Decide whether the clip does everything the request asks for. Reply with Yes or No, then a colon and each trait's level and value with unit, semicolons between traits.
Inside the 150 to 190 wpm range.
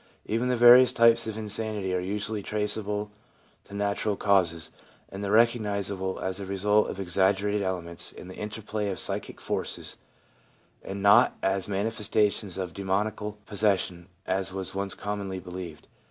No: average, 140 wpm